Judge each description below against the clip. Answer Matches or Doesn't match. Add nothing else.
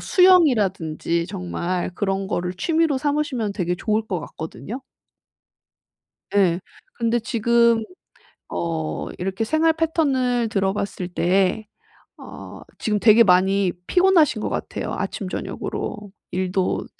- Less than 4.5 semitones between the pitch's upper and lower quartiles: Doesn't match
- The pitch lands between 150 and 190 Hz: Doesn't match